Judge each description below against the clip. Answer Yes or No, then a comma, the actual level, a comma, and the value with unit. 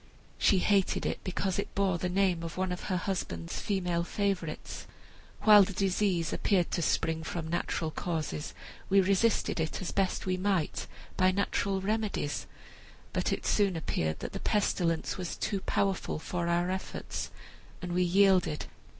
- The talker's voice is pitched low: No, medium, 185 Hz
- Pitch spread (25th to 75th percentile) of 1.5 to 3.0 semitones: Yes, narrow, 2.6 semitones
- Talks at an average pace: Yes, average, 160 wpm